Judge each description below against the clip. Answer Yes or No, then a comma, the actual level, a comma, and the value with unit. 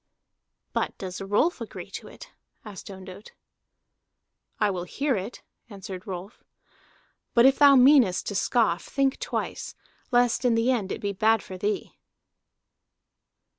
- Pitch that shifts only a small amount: No, average, 4.5 semitones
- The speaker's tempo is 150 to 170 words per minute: No, slow, 135 wpm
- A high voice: Yes, high, 210 Hz